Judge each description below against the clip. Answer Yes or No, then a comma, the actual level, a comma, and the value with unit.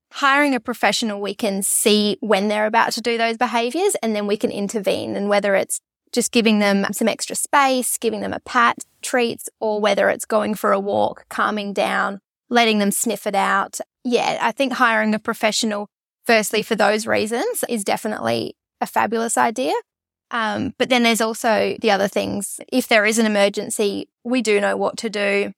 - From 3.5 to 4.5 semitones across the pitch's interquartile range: No, narrow, 2.5 semitones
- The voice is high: Yes, high, 220 Hz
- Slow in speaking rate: No, average, 190 wpm